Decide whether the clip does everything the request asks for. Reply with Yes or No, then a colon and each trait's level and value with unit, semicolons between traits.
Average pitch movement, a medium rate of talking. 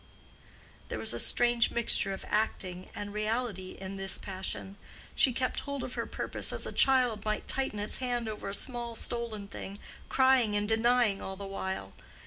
Yes: average, 3.5 semitones; average, 175 wpm